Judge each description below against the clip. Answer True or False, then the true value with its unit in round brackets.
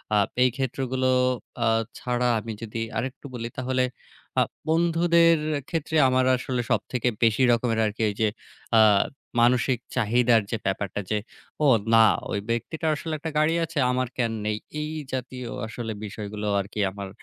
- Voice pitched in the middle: False (125 Hz)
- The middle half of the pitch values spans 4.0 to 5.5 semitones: False (3.1 semitones)